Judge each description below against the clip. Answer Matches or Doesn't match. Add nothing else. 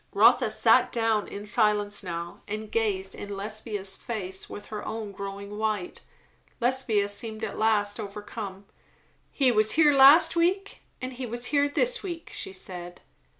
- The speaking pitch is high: Matches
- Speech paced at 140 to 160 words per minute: Matches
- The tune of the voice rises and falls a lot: Doesn't match